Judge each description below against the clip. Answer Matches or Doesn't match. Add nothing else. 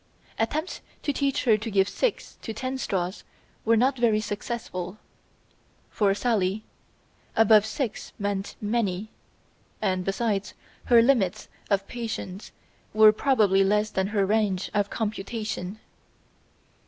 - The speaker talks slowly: Matches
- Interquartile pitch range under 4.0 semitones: Matches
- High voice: Matches